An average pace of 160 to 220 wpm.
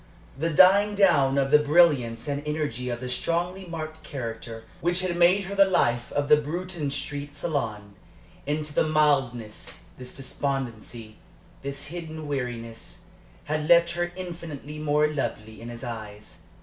No: average, 150 wpm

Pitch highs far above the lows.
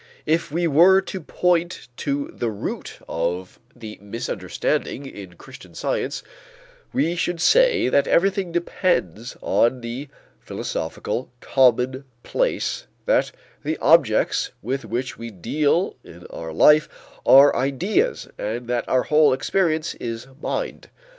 Yes: wide, 6.5 semitones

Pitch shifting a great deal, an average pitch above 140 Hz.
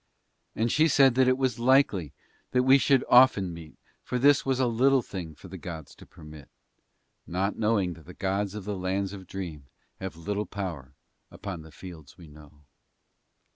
No: wide, 6.9 semitones; very low, 95 Hz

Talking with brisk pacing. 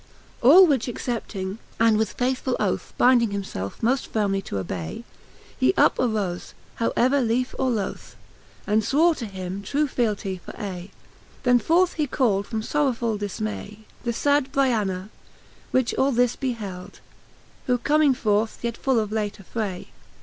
No: average, 155 wpm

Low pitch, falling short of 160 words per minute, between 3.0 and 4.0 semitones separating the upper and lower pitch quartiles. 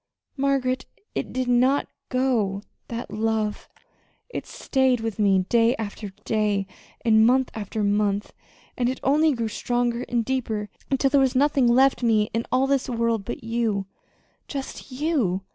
No: high, 235 Hz; average, 150 wpm; average, 3.5 semitones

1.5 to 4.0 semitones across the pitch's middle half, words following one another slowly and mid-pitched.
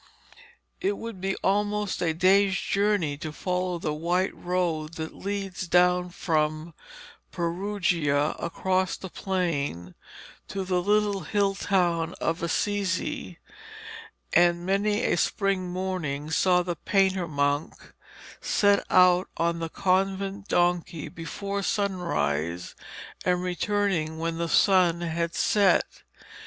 Yes: average, 2.9 semitones; slow, 115 wpm; medium, 180 Hz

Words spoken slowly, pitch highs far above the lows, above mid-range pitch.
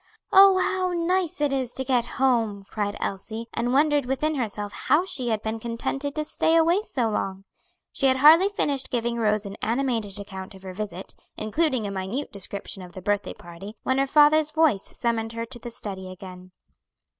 No: average, 190 wpm; wide, 6.2 semitones; high, 235 Hz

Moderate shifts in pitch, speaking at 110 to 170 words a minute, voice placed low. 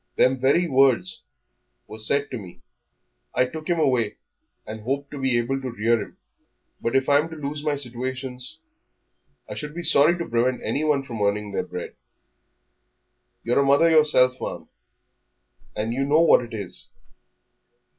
Yes: average, 3.7 semitones; average, 165 wpm; low, 130 Hz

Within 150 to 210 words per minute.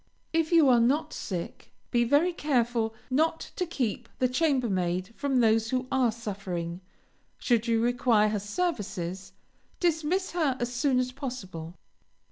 No: average, 140 wpm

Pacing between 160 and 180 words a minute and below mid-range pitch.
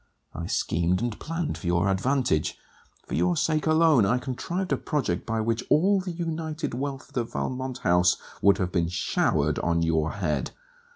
Yes: average, 175 wpm; low, 120 Hz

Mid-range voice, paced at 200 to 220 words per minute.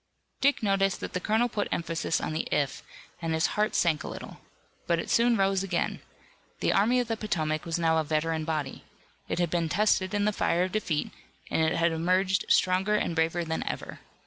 Yes: medium, 175 Hz; fast, 205 wpm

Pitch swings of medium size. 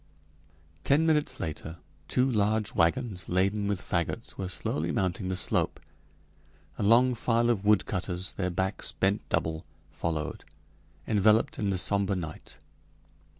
Yes: average, 3.5 semitones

